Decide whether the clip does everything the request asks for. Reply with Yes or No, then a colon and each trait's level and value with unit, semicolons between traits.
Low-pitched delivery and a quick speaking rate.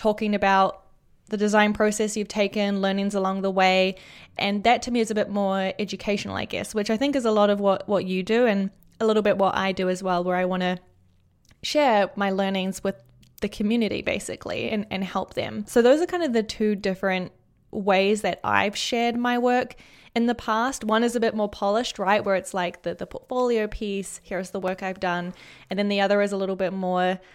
No: high, 200 Hz; fast, 225 wpm